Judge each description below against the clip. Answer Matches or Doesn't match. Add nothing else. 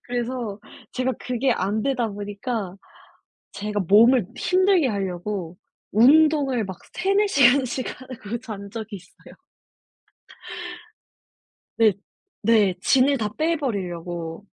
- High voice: Matches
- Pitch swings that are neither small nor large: Matches